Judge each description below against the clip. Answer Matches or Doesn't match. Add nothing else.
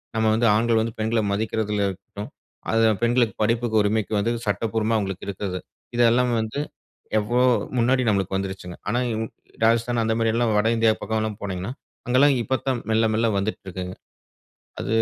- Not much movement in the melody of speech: Matches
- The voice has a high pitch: Doesn't match